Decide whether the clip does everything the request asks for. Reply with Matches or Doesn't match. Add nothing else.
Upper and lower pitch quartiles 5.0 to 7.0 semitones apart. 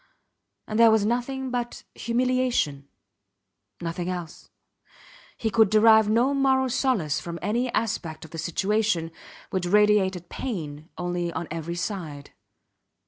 Matches